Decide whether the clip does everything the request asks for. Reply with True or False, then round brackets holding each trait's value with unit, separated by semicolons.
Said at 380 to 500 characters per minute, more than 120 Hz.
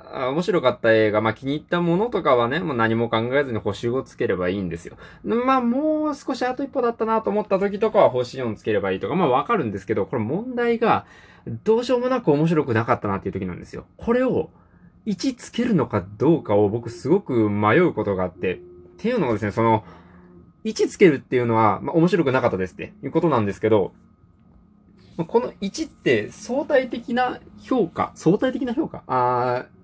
True (395 characters per minute; 140 Hz)